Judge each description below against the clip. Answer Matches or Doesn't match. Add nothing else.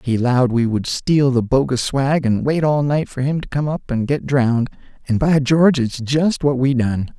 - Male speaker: Matches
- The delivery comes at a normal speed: Doesn't match